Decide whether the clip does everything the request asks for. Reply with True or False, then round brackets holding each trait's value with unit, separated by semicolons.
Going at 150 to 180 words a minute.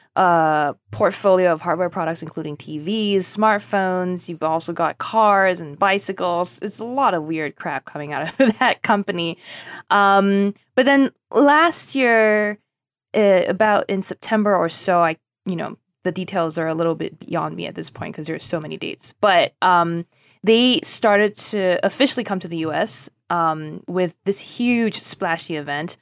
True (165 wpm)